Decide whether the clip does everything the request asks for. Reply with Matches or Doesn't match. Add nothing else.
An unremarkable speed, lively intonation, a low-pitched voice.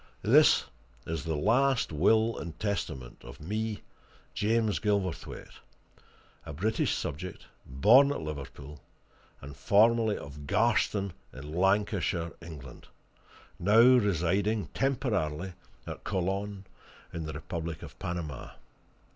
Doesn't match